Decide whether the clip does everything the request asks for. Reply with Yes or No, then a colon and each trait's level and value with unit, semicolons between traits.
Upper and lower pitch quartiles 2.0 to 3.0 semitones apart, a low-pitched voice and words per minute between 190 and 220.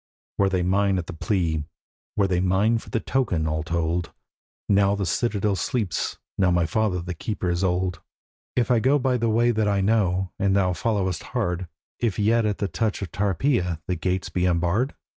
No: average, 3.6 semitones; very low, 95 Hz; average, 195 wpm